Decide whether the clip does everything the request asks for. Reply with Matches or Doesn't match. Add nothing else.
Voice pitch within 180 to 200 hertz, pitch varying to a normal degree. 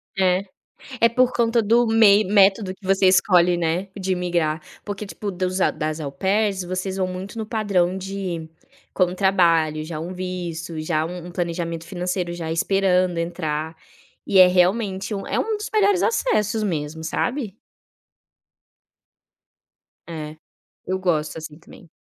Matches